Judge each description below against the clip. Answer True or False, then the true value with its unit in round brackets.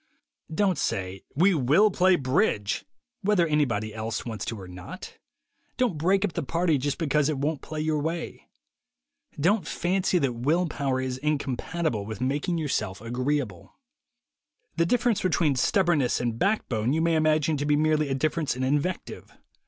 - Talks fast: False (165 wpm)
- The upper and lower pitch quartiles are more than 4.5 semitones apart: True (5.1 semitones)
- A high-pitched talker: False (150 Hz)